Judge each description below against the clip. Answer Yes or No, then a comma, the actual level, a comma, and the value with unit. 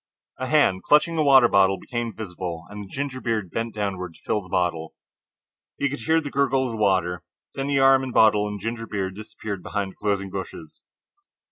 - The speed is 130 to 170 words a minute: No, average, 200 wpm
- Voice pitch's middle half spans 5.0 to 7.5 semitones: Yes, wide, 5.6 semitones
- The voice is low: Yes, low, 105 Hz